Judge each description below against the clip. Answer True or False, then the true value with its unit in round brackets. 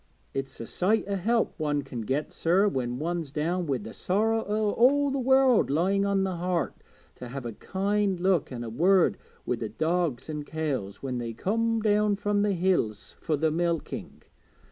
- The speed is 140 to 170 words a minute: False (185 wpm)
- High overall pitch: False (175 Hz)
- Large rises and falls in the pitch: True (6.8 semitones)